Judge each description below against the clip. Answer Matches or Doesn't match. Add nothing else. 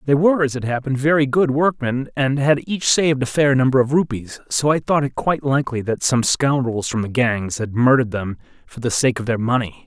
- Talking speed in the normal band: Doesn't match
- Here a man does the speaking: Matches